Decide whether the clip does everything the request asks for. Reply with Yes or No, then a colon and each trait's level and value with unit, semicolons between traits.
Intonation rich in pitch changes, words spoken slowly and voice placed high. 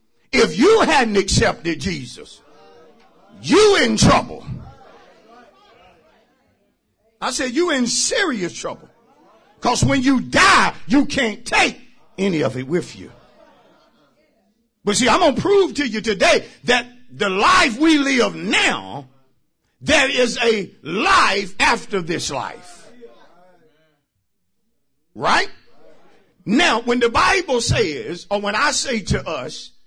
Yes: wide, 6.6 semitones; slow, 120 wpm; high, 235 Hz